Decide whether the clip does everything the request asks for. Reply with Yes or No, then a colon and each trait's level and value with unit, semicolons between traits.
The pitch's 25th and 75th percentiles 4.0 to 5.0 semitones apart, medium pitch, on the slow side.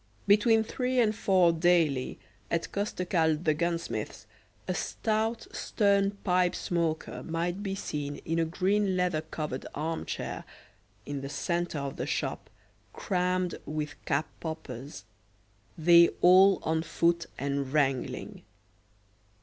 No: average, 3.6 semitones; medium, 170 Hz; slow, 125 wpm